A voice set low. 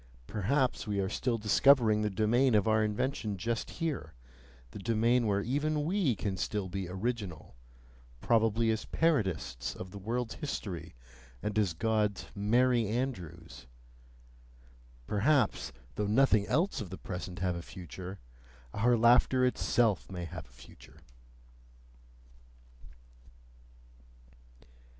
Yes: low, 105 Hz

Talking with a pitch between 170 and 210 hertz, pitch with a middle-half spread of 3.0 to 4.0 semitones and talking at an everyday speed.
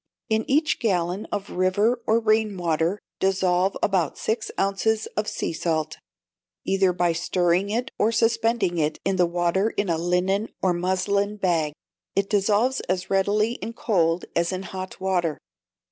Yes: high, 190 Hz; average, 3.3 semitones; average, 155 wpm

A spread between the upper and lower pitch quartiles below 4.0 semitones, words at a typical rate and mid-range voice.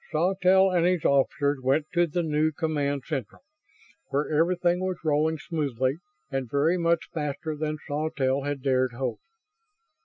Yes: average, 3.3 semitones; average, 145 wpm; medium, 150 Hz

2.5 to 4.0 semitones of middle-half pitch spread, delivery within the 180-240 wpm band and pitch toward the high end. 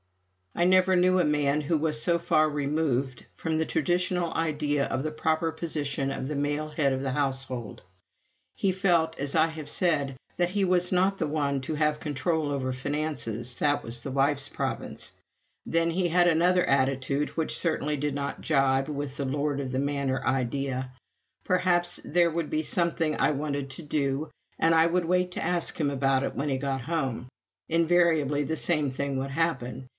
No: average, 3.3 semitones; average, 185 wpm; medium, 150 Hz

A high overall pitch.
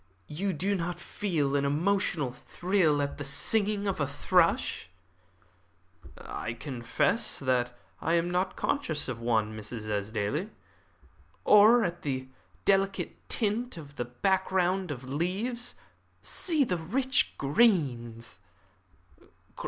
No: medium, 165 Hz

